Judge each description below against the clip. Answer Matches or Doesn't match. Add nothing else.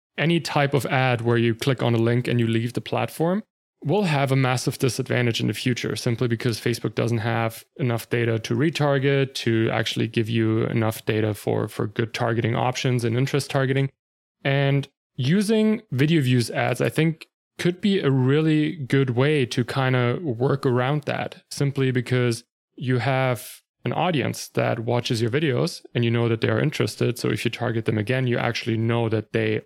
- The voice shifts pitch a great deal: Doesn't match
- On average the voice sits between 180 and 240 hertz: Doesn't match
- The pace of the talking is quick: Doesn't match